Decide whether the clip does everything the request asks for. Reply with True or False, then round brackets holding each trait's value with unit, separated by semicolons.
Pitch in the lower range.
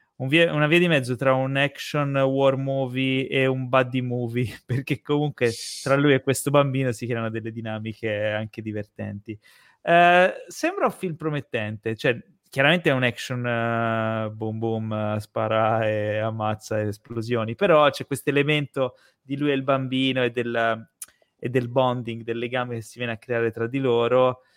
True (125 Hz)